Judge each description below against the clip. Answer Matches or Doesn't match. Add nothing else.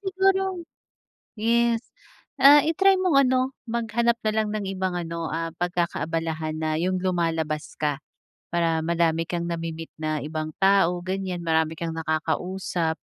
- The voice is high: Doesn't match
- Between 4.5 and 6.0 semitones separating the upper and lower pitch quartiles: Matches